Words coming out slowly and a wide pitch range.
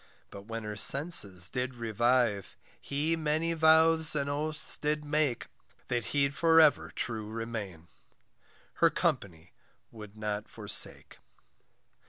Yes: slow, 120 wpm; wide, 6.2 semitones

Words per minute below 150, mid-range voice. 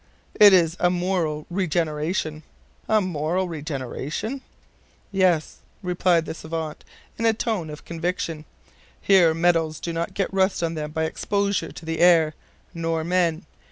Yes: average, 140 wpm; medium, 170 Hz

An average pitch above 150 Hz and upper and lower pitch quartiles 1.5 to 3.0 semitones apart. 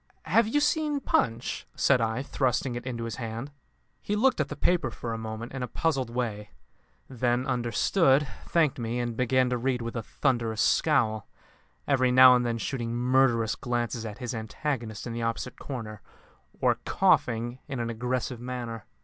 No: low, 120 Hz; narrow, 2.4 semitones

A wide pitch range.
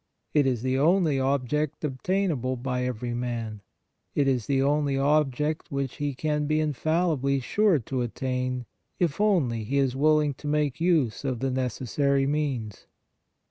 No: average, 3.0 semitones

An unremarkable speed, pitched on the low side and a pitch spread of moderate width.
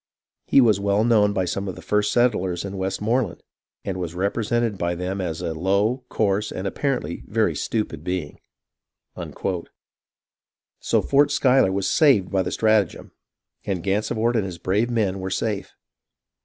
Yes: average, 160 wpm; low, 100 Hz; average, 3.3 semitones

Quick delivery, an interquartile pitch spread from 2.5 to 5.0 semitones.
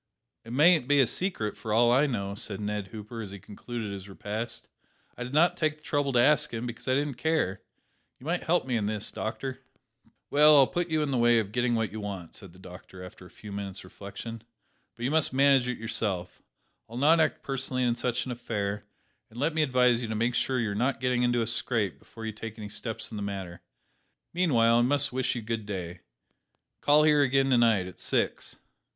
Yes: fast, 225 wpm; average, 4.5 semitones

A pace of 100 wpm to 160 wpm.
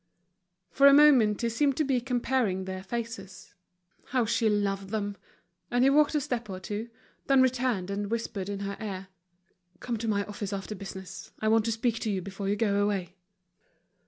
No: average, 190 wpm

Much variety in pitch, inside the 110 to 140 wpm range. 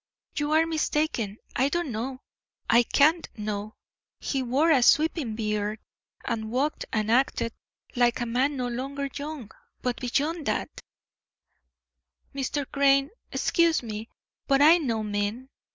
No: average, 4.4 semitones; slow, 135 wpm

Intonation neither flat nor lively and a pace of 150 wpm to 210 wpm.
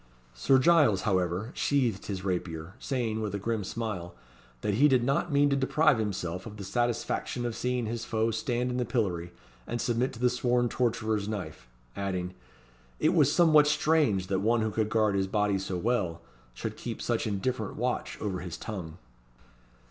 Yes: average, 4.3 semitones; average, 180 wpm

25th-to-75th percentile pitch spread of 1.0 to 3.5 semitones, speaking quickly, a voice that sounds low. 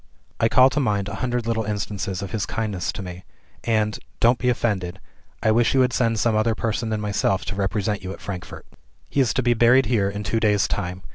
Yes: average, 2.9 semitones; fast, 225 wpm; low, 110 Hz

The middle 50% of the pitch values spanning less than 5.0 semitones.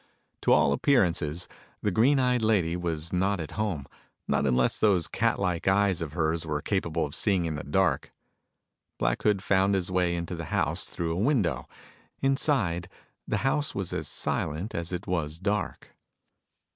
Yes: average, 3.9 semitones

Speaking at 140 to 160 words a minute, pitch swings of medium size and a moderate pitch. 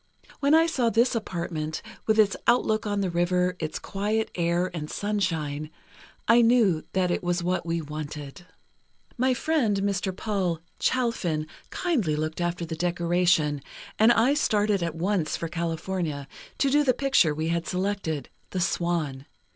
Yes: average, 155 wpm; average, 4.9 semitones; medium, 180 Hz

